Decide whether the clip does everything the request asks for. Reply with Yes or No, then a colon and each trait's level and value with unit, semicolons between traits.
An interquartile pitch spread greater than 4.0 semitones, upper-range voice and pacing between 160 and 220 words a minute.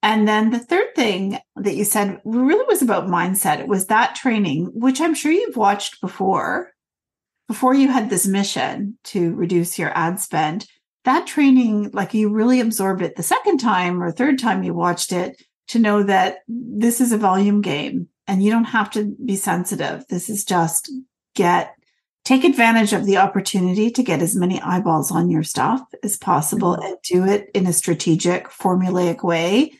Yes: average, 4.6 semitones; high, 205 Hz; average, 180 wpm